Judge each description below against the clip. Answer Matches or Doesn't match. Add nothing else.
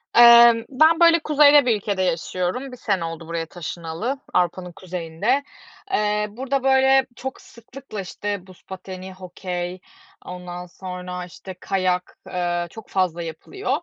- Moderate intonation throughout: Doesn't match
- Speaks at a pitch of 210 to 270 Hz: Doesn't match